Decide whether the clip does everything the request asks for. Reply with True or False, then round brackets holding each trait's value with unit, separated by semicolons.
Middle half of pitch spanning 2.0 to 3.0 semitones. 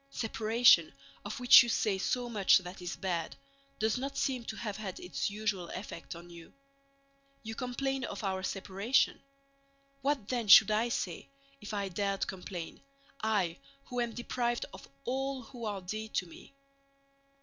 False (4.2 semitones)